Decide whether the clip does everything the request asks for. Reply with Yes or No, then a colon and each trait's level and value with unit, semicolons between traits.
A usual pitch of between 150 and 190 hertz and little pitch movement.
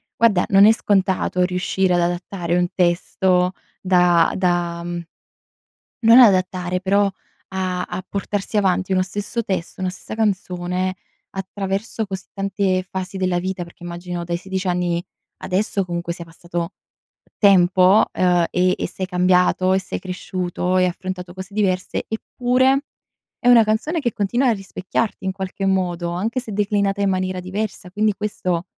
Yes: medium, 185 Hz; narrow, 2.0 semitones